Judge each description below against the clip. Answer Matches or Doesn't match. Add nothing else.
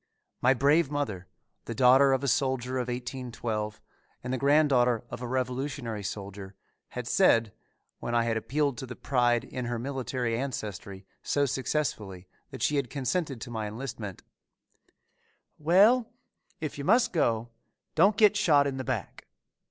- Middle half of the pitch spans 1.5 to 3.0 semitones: Doesn't match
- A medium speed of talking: Matches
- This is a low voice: Matches